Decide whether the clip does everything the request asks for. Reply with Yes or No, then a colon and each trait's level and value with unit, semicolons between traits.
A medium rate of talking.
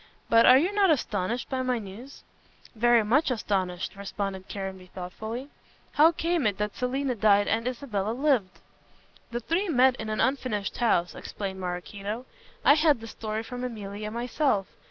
Yes: average, 155 wpm